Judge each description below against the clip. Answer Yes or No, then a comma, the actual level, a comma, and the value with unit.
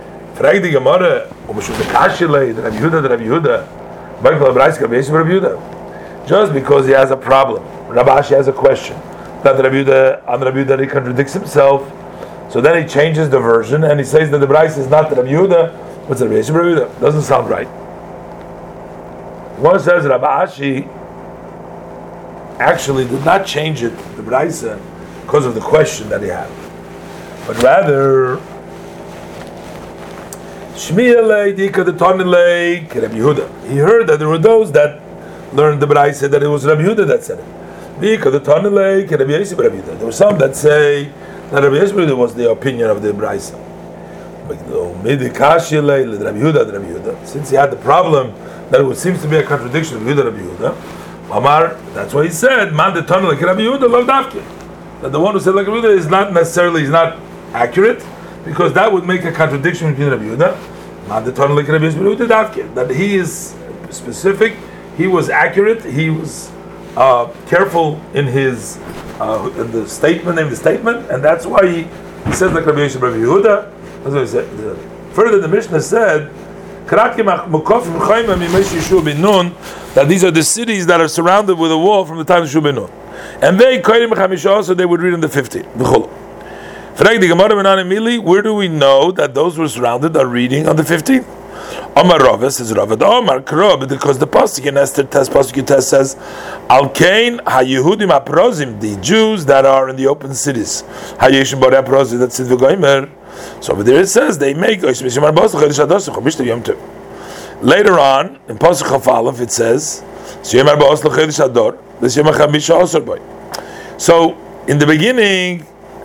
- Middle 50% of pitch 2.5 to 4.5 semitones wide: No, wide, 5.6 semitones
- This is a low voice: No, medium, 165 Hz